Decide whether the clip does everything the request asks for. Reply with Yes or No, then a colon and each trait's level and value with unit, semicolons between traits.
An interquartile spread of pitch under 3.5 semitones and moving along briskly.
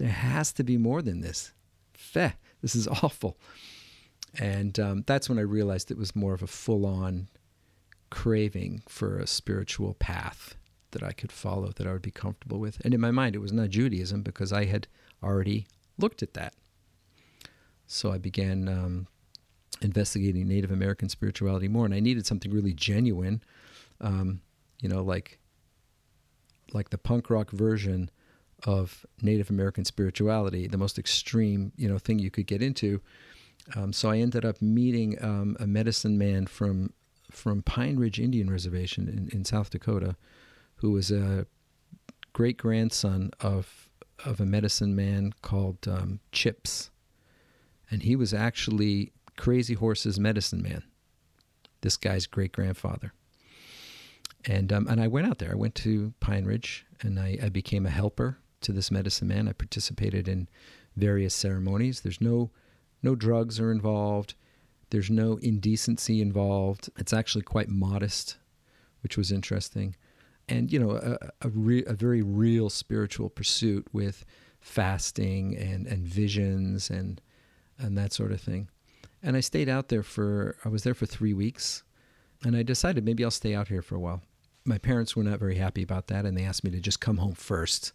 No: average, 2.7 semitones; average, 165 wpm